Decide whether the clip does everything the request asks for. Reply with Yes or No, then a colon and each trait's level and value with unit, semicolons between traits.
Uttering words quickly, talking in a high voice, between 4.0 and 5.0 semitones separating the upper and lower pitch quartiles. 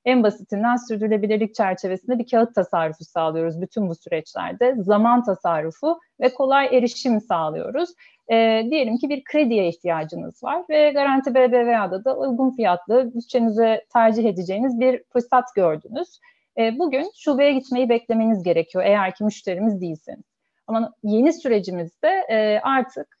No: average, 130 wpm; high, 230 Hz; average, 4.4 semitones